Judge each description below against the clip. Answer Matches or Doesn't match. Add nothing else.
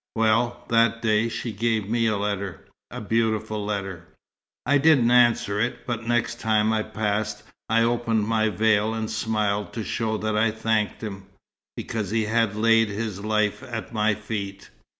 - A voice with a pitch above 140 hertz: Doesn't match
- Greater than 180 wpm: Doesn't match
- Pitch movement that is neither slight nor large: Doesn't match